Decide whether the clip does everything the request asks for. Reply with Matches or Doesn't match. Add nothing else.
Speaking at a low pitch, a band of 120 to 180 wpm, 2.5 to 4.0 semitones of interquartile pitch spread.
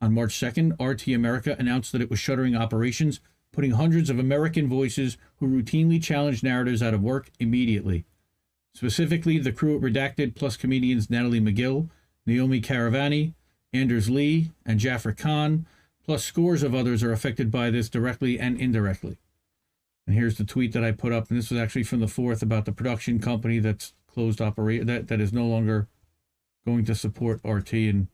Matches